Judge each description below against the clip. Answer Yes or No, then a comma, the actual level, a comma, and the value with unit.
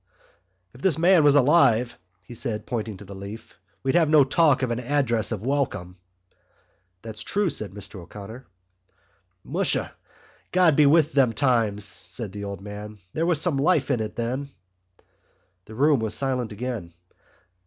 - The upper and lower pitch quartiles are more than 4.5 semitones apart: Yes, average, 5.3 semitones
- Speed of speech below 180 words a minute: Yes, average, 160 wpm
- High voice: No, low, 120 Hz